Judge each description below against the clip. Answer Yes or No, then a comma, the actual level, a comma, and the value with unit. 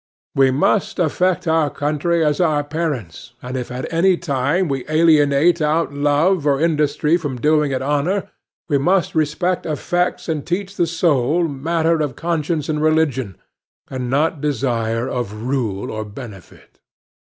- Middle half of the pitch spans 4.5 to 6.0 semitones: No, average, 3.8 semitones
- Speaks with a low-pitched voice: No, medium, 150 Hz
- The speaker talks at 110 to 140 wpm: No, average, 150 wpm